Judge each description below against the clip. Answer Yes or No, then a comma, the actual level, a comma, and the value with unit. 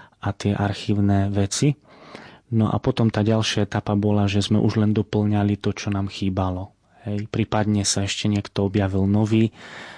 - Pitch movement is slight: Yes, narrow, 1.2 semitones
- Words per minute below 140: No, average, 160 wpm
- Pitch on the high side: No, low, 105 Hz